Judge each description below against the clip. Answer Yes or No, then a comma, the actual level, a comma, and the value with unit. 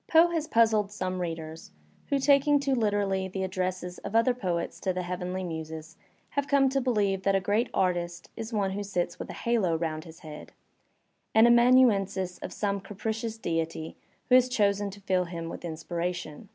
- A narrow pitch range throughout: No, average, 4.5 semitones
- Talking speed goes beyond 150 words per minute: Yes, average, 180 wpm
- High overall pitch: Yes, high, 195 Hz